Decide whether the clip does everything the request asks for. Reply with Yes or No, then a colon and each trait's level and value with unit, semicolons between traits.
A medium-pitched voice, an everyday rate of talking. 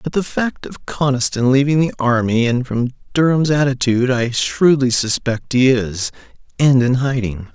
No: low, 125 Hz; average, 160 wpm